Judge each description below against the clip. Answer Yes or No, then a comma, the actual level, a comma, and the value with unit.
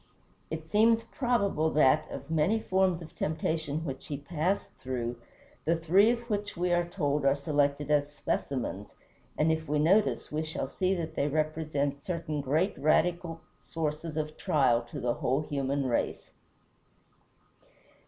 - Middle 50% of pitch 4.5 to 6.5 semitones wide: No, average, 3.4 semitones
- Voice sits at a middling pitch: Yes, medium, 155 Hz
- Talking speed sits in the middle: Yes, average, 150 wpm